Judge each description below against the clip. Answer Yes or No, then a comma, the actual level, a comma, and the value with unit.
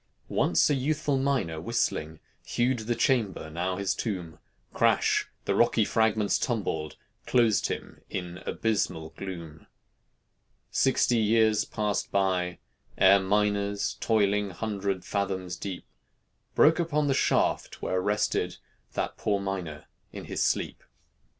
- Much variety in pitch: No, average, 3.7 semitones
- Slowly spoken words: Yes, slow, 120 wpm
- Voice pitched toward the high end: No, low, 100 Hz